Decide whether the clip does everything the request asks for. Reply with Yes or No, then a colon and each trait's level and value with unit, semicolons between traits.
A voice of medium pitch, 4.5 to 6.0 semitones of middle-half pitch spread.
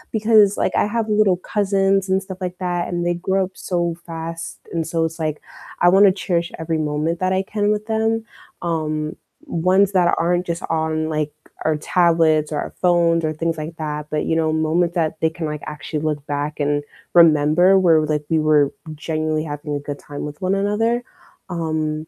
No: medium, 165 Hz; average, 3.1 semitones